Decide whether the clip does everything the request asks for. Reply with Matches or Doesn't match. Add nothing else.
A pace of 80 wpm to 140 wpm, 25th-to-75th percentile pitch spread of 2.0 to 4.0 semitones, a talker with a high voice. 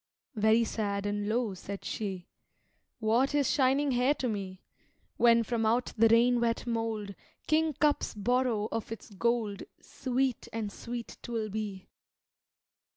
Matches